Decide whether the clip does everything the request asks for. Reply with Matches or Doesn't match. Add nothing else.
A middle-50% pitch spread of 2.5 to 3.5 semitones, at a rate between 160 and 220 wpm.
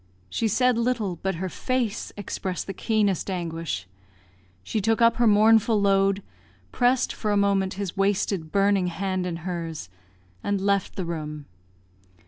Doesn't match